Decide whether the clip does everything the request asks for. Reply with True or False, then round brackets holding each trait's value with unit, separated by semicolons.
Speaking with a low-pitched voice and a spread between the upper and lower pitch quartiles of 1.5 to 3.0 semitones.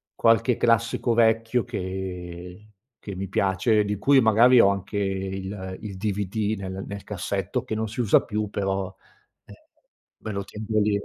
True (100 Hz; 2.5 semitones)